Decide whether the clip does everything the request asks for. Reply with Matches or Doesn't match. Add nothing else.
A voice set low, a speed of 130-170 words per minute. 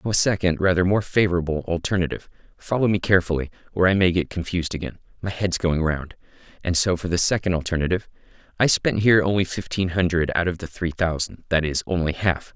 Doesn't match